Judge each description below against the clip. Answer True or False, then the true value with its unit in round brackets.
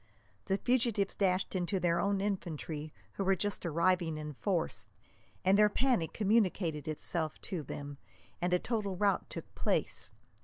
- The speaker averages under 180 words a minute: True (150 wpm)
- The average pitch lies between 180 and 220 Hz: True (185 Hz)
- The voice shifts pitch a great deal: False (3.7 semitones)